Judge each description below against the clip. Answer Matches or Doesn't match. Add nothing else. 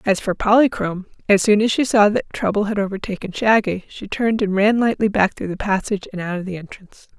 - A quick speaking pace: Matches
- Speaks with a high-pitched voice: Matches